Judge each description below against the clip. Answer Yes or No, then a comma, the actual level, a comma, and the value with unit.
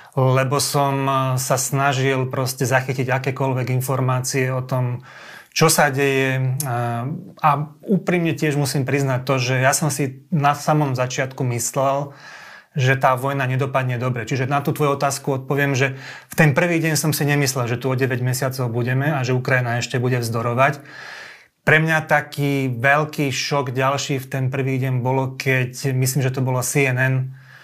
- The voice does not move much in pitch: Yes, narrow, 1.7 semitones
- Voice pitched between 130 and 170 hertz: Yes, low, 135 Hz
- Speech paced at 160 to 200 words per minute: Yes, fast, 165 wpm